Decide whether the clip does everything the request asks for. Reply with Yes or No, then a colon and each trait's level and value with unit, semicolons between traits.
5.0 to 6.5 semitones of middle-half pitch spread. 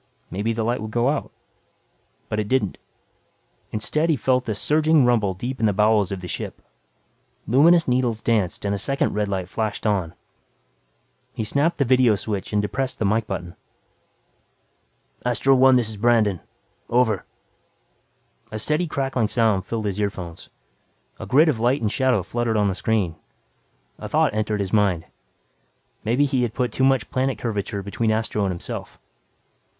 No: average, 3.8 semitones